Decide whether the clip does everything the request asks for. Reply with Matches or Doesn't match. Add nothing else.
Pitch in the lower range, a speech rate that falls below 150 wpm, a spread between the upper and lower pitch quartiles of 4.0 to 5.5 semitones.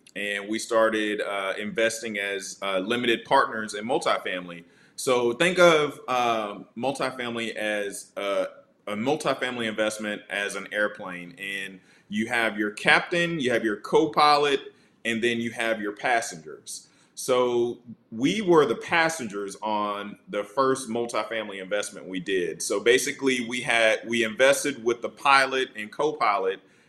Matches